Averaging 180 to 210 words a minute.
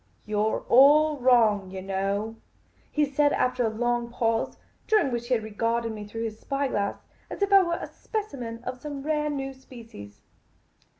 Yes: average, 185 wpm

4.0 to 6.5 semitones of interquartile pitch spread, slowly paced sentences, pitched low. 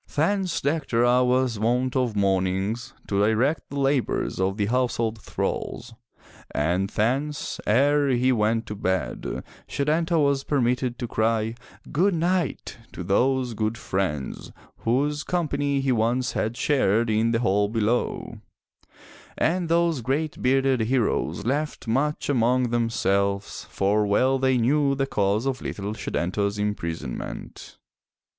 Yes: average, 4.6 semitones; slow, 130 wpm; low, 120 Hz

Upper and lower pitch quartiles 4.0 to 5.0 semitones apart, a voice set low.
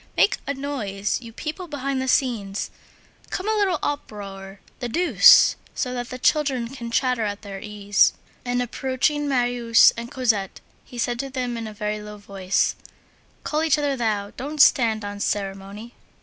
No: average, 4.6 semitones; high, 240 Hz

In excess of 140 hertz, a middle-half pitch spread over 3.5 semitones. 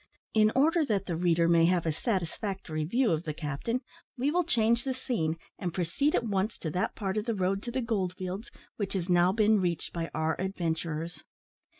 Yes: high, 190 Hz; average, 5.2 semitones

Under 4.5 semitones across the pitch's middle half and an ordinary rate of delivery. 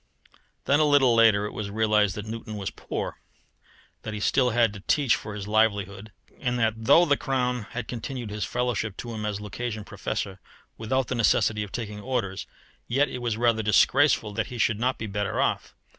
Yes: average, 2.9 semitones; average, 195 wpm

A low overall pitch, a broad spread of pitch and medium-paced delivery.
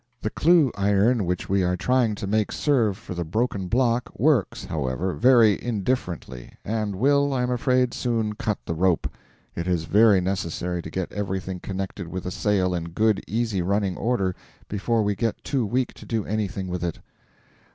No: low, 100 Hz; average, 4.4 semitones; average, 180 wpm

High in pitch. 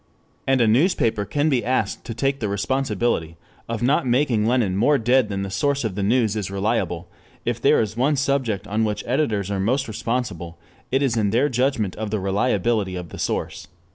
No: low, 115 Hz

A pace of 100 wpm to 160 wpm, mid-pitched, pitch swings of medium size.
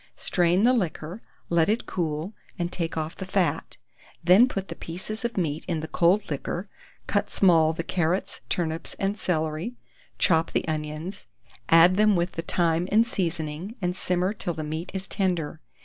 No: average, 170 wpm; medium, 175 Hz; average, 3.2 semitones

